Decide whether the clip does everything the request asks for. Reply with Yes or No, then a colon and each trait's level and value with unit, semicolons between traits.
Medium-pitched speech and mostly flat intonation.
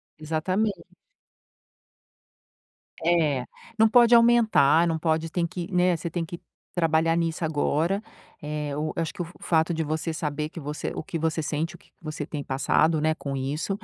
Yes: medium, 160 Hz; narrow, 2.1 semitones